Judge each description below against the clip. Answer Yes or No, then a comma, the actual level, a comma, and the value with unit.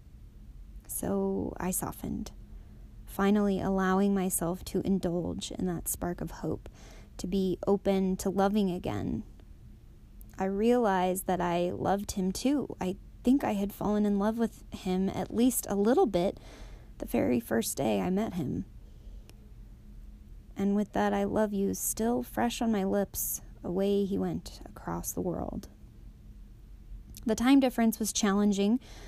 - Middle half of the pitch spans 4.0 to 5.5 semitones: No, narrow, 2.5 semitones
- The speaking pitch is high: Yes, high, 195 Hz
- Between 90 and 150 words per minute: Yes, average, 140 wpm